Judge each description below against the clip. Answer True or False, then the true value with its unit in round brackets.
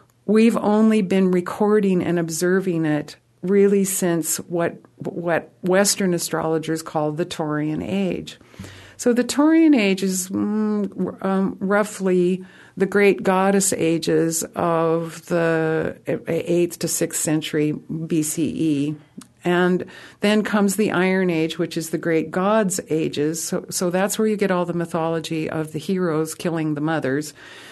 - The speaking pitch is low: False (175 Hz)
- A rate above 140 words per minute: False (135 wpm)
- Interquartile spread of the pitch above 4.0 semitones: False (3.3 semitones)